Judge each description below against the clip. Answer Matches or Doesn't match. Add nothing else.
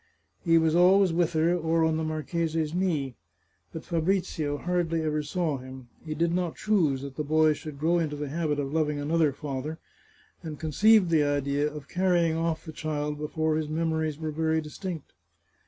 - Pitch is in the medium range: Matches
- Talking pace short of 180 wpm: Doesn't match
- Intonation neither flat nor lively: Doesn't match